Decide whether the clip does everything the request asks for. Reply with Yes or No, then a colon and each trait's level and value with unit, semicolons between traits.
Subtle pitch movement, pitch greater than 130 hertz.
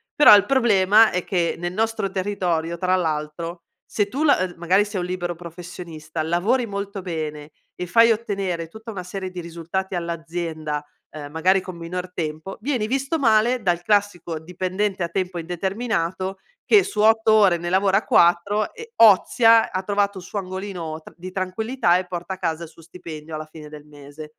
No: average, 3.5 semitones; medium, 185 Hz